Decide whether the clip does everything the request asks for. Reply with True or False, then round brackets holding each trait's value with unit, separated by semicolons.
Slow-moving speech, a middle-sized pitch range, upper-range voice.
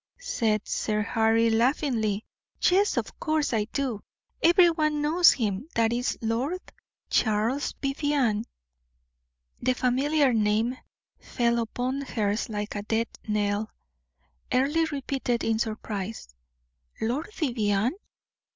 True (115 wpm; 4.5 semitones; 235 Hz)